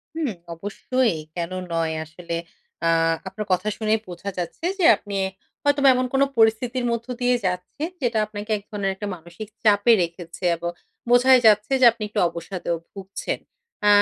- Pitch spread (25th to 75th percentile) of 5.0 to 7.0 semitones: Yes, average, 5.3 semitones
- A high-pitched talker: Yes, high, 210 Hz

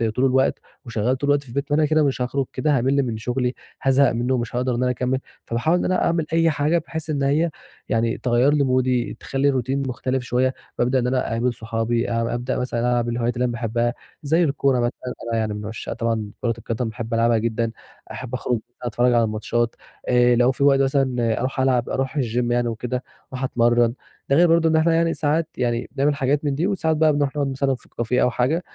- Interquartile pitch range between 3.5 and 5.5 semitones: No, average, 2.9 semitones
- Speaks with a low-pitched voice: Yes, low, 125 Hz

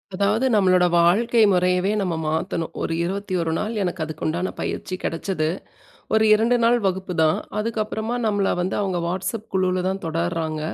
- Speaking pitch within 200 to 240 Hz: No, medium, 185 Hz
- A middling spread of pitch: Yes, average, 3.4 semitones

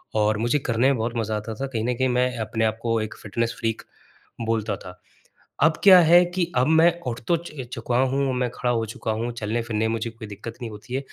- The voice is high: No, low, 115 Hz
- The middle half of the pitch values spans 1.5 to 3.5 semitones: Yes, average, 2.9 semitones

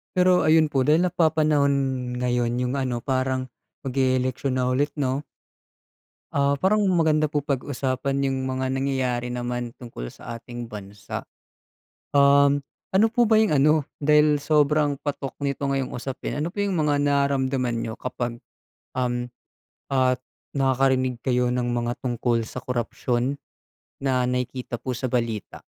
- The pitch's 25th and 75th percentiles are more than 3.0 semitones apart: No, average, 2.7 semitones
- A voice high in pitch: No, low, 130 Hz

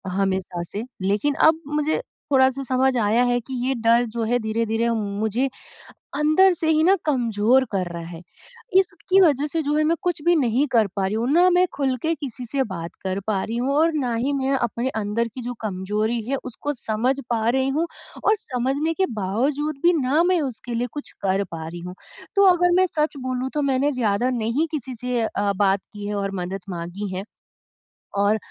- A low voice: No, high, 245 Hz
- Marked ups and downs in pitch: Yes, wide, 5.8 semitones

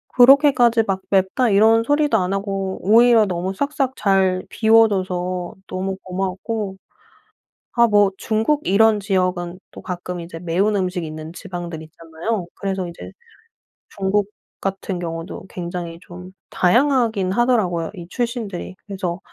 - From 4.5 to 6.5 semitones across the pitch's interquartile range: No, average, 3.7 semitones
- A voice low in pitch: No, high, 195 Hz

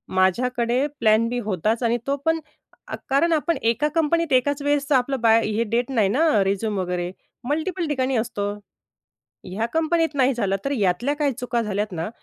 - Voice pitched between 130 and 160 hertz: No, high, 245 Hz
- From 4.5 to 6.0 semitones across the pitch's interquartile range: Yes, average, 5.1 semitones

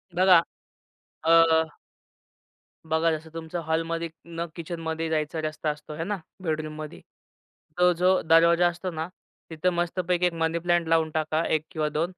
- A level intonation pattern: Yes, narrow, 1.5 semitones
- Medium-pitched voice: Yes, medium, 165 Hz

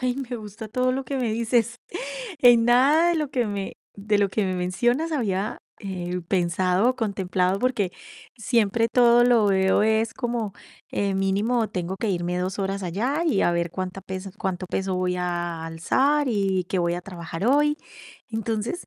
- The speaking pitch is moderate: No, high, 205 Hz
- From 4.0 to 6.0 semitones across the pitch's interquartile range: Yes, average, 4.6 semitones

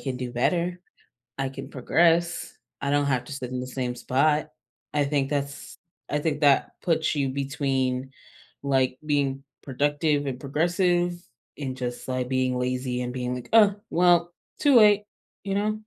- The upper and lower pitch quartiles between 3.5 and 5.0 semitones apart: Yes, average, 4.2 semitones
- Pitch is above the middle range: No, medium, 140 Hz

